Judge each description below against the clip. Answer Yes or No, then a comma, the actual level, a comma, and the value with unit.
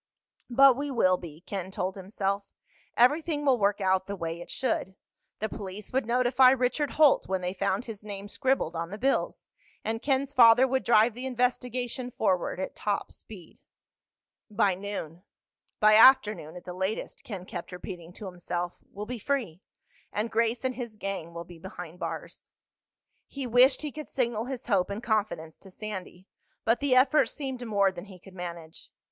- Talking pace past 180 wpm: No, average, 175 wpm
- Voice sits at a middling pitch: No, high, 210 Hz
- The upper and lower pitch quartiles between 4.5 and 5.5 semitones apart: Yes, average, 5.2 semitones